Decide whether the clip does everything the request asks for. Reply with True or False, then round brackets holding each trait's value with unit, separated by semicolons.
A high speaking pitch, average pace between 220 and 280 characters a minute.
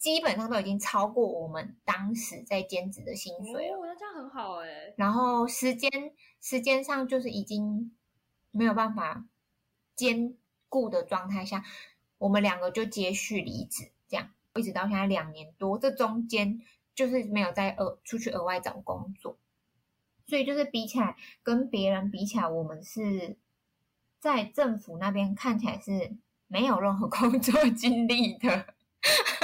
True (220 Hz; 235 characters per minute)